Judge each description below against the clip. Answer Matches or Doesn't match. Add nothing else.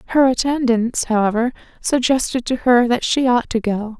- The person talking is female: Matches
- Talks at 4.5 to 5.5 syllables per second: Matches